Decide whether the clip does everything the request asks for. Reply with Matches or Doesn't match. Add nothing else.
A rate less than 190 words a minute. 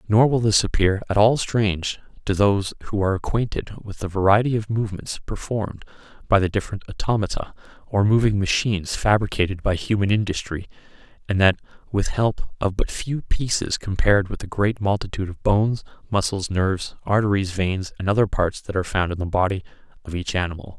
Matches